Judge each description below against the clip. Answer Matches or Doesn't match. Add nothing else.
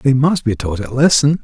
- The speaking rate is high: Matches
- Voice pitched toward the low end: Matches